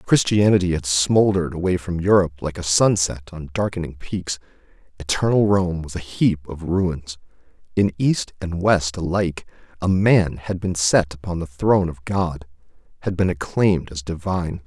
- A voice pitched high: No, very low, 90 Hz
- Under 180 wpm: Yes, average, 160 wpm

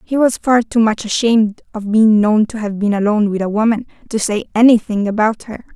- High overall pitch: Yes, high, 220 Hz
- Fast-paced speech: Yes, fast, 220 wpm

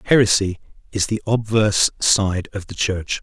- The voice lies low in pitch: Yes, low, 100 Hz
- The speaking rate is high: No, average, 150 wpm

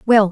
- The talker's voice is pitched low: No, high, 210 Hz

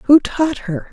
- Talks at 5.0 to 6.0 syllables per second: No, 3.5 syllables/s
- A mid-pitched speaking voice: No, very high, 255 Hz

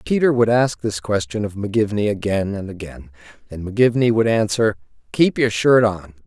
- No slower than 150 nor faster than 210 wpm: Yes, average, 170 wpm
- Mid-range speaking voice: No, low, 105 Hz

